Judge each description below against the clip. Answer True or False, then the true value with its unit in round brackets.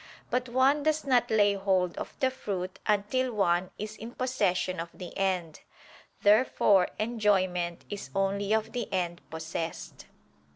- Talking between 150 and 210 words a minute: False (140 wpm)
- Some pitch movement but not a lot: True (4.6 semitones)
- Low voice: False (200 Hz)